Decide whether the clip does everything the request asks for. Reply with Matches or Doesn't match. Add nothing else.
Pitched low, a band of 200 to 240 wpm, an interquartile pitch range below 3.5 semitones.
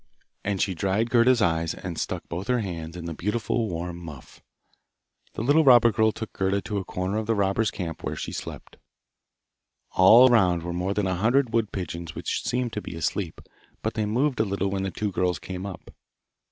Doesn't match